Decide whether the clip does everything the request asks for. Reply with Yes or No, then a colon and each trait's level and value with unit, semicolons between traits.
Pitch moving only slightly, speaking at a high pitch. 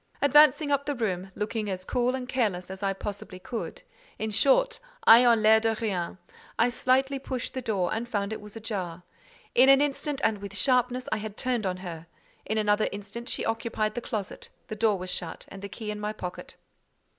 No: average, 3.9 semitones; high, 220 Hz